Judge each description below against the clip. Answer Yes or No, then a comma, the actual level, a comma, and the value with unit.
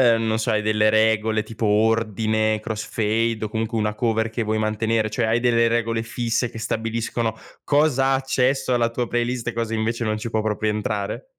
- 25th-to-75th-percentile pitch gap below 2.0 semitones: Yes, narrow, 1.3 semitones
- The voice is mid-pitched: No, low, 115 Hz